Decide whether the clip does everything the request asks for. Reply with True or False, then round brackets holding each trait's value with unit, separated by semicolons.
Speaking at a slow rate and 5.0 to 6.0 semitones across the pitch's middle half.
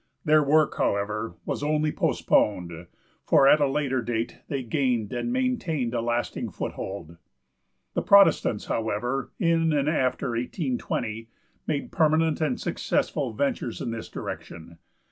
True (130 wpm; 5.3 semitones)